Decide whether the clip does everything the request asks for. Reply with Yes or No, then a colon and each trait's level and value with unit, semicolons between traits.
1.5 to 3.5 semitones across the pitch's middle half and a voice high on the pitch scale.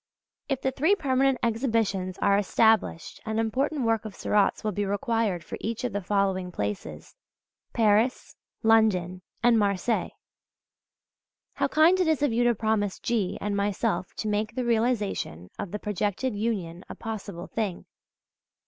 Yes: average, 3.1 semitones; high, 215 Hz